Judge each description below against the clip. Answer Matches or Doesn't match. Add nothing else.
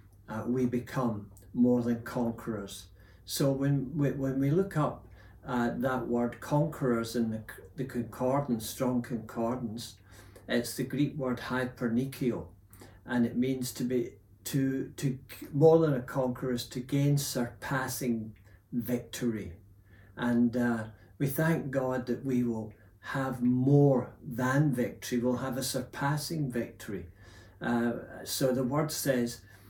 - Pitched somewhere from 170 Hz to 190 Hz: Doesn't match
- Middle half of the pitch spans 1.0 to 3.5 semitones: Matches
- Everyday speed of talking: Doesn't match